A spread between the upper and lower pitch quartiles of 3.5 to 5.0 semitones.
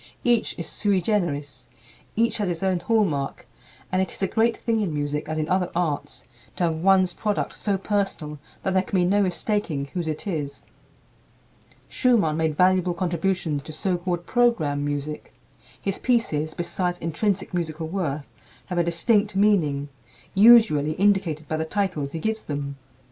Yes: average, 4.6 semitones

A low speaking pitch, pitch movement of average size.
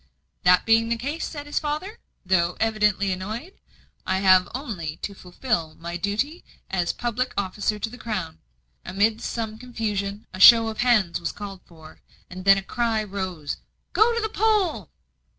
No: high, 210 Hz; average, 4.4 semitones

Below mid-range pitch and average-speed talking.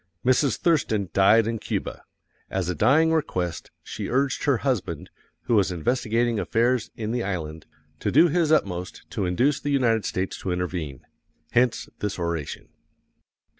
Yes: low, 110 Hz; average, 150 wpm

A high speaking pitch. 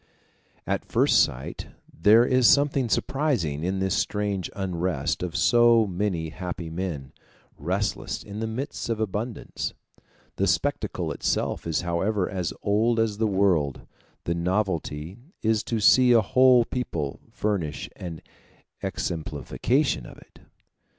No: low, 100 Hz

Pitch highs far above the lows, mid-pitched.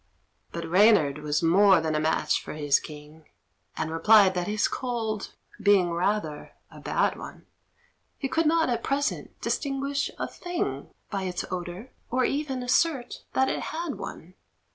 No: wide, 8.2 semitones; high, 205 Hz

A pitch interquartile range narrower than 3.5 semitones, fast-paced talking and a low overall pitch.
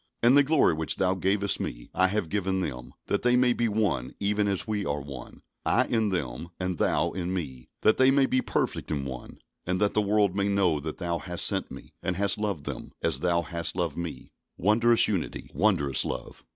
No: average, 4.2 semitones; fast, 215 wpm; very low, 95 Hz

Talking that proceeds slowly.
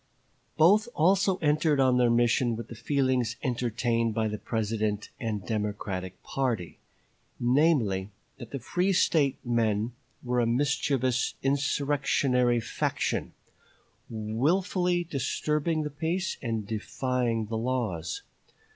Yes: slow, 110 wpm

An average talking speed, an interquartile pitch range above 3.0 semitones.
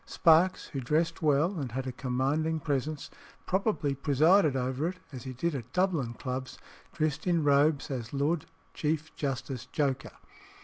Yes: average, 150 wpm; average, 3.5 semitones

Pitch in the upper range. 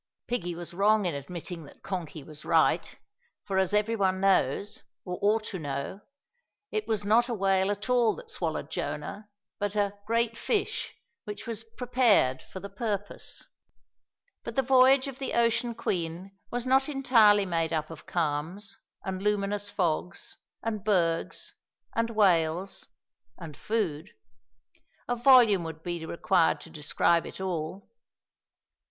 Yes: high, 200 Hz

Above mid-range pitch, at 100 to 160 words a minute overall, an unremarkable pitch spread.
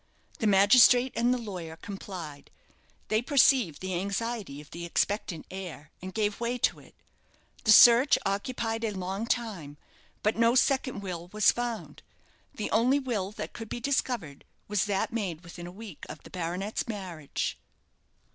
Yes: high, 205 Hz; average, 155 wpm; average, 4.5 semitones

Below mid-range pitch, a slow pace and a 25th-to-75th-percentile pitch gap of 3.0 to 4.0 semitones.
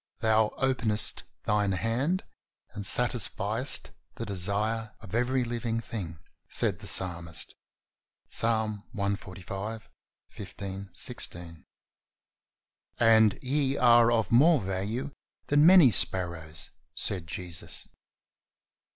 Yes: low, 110 Hz; slow, 95 wpm; average, 3.6 semitones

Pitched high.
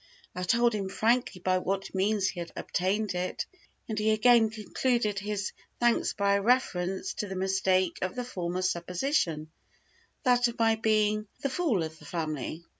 Yes: high, 200 Hz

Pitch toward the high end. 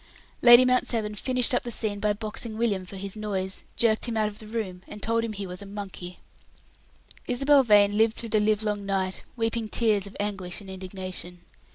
Yes: high, 210 Hz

